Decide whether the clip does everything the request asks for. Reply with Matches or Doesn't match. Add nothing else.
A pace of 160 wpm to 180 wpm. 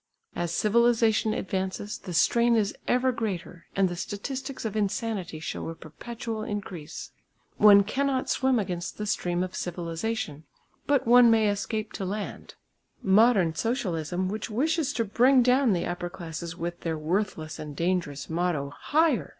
Doesn't match